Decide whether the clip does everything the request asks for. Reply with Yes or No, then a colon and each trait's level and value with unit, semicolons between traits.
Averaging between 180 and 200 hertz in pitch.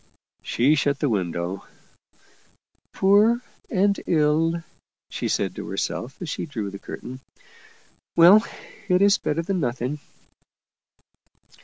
No: medium, 155 Hz